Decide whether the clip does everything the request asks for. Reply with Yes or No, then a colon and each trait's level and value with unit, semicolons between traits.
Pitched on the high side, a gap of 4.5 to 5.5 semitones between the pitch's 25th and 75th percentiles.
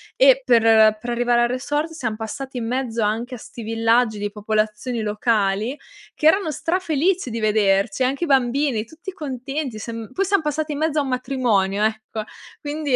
Yes: high, 245 Hz; average, 5.2 semitones